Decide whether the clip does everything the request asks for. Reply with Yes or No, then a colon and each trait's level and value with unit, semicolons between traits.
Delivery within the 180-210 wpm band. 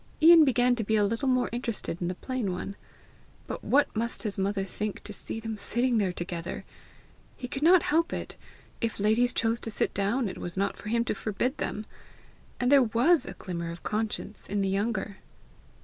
Yes: average, 200 wpm